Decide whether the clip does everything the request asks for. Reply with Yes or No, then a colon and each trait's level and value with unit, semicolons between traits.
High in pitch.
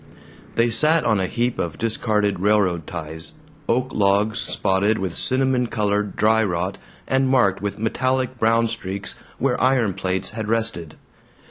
No: low, 110 Hz